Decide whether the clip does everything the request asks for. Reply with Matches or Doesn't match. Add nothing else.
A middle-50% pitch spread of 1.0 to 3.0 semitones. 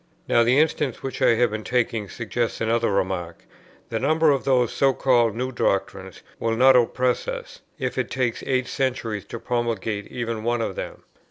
Matches